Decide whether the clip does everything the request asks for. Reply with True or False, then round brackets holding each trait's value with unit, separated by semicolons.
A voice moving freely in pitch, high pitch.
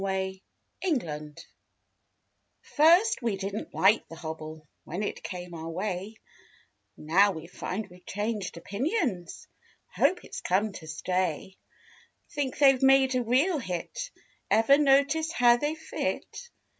True (7.2 semitones; 205 Hz)